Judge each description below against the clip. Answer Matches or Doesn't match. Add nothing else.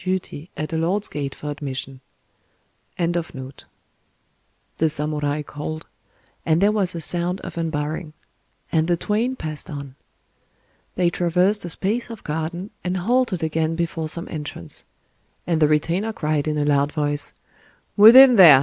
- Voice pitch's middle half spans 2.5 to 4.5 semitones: Matches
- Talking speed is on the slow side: Matches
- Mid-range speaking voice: Matches